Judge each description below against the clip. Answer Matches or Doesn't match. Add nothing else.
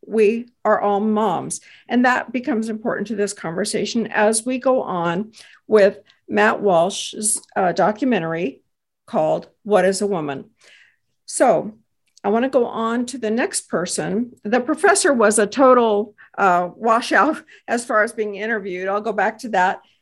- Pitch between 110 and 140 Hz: Doesn't match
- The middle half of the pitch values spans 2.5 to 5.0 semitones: Matches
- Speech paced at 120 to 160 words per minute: Matches